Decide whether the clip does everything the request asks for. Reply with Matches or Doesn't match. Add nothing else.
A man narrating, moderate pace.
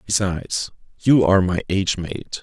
Matches